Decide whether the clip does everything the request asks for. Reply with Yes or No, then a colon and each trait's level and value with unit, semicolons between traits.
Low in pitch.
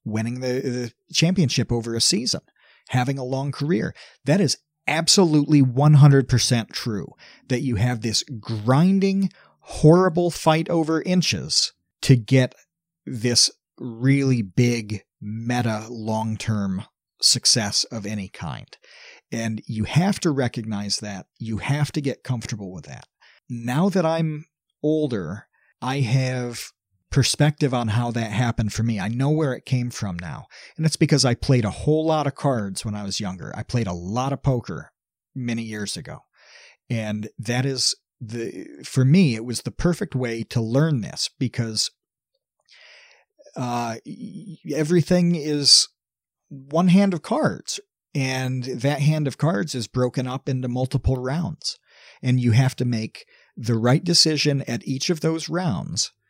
Yes: low, 130 Hz